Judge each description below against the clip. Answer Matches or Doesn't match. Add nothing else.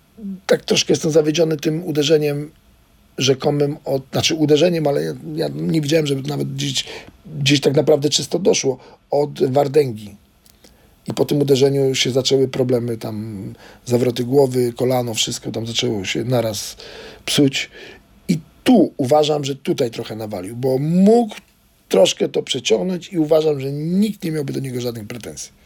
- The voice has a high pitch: Doesn't match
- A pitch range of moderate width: Matches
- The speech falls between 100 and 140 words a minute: Doesn't match